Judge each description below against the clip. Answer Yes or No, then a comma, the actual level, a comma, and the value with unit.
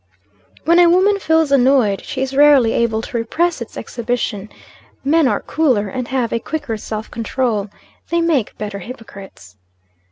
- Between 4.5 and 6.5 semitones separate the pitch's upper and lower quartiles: Yes, average, 5.2 semitones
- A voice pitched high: Yes, very high, 250 Hz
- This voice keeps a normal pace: Yes, average, 155 wpm